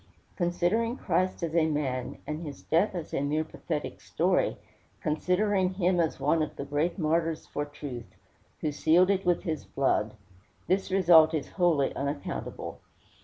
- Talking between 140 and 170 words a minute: Yes, average, 155 wpm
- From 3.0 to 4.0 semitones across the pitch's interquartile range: Yes, average, 3.5 semitones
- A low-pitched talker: No, medium, 165 Hz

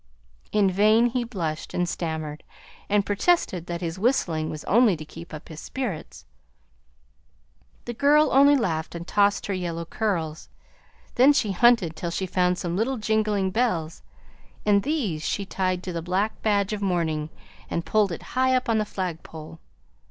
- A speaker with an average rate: Yes, average, 165 wpm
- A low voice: No, high, 190 Hz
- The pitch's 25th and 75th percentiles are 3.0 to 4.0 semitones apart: No, average, 4.8 semitones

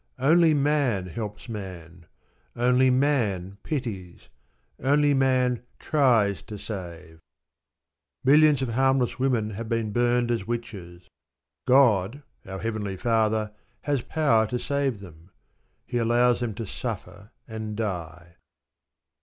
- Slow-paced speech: Yes, slow, 115 wpm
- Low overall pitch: Yes, low, 115 Hz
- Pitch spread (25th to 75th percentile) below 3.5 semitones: No, average, 4.7 semitones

